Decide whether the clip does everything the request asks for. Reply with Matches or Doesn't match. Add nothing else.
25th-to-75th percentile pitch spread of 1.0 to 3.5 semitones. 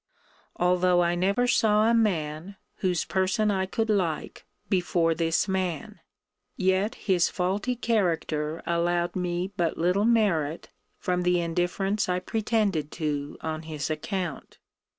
Matches